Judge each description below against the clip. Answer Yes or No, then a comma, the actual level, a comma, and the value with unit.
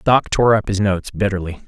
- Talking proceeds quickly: Yes, fast, 215 wpm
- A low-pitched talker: Yes, low, 100 Hz